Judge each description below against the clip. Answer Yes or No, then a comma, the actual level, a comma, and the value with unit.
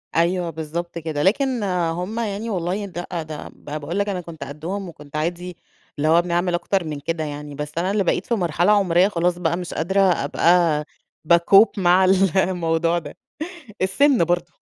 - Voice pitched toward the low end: No, medium, 175 Hz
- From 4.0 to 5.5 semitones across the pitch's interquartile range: No, average, 2.8 semitones